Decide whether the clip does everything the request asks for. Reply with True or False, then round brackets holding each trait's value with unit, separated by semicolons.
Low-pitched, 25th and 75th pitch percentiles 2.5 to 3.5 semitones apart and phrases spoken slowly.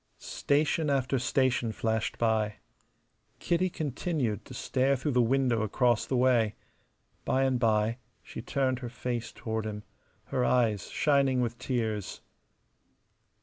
True (125 Hz; 3.1 semitones; 125 wpm)